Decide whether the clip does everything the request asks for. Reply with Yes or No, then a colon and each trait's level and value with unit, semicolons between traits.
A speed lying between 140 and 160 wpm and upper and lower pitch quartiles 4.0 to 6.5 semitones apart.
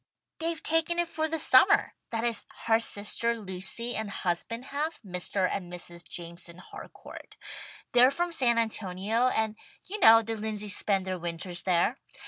Yes: average, 155 wpm; wide, 5.6 semitones